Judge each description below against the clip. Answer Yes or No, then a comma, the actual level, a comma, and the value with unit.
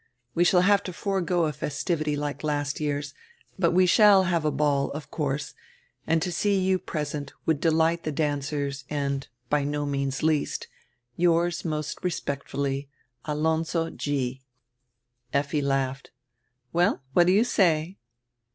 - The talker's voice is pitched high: No, medium, 155 Hz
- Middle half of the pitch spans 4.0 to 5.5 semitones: No, average, 3.3 semitones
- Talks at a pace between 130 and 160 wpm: Yes, average, 140 wpm